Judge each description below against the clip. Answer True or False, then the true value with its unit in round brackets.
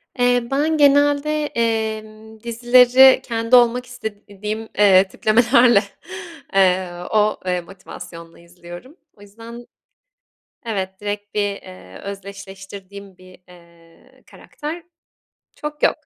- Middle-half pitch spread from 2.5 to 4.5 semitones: True (4.2 semitones)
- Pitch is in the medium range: False (215 Hz)